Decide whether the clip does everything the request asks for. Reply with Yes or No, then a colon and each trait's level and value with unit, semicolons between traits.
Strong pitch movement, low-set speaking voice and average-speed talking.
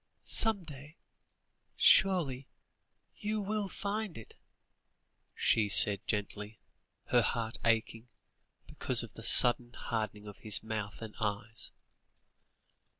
No: wide, 8.5 semitones; low, 115 Hz; slow, 105 wpm